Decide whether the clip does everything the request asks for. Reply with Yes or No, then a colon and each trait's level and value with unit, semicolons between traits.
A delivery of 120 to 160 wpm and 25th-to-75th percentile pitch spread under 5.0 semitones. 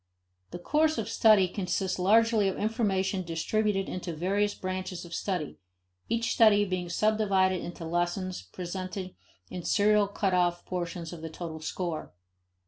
Yes: slow, 135 wpm; average, 3.0 semitones